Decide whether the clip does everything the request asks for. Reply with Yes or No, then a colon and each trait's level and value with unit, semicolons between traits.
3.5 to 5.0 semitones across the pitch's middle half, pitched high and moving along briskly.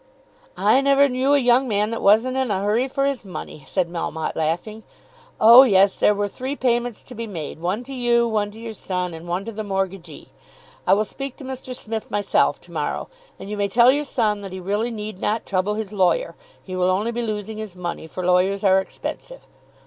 Yes: average, 4.1 semitones; high, 210 Hz; fast, 215 wpm